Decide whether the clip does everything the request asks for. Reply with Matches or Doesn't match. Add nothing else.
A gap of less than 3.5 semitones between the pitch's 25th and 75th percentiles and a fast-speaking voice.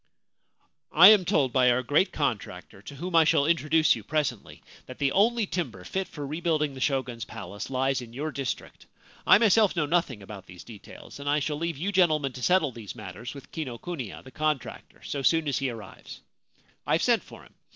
Doesn't match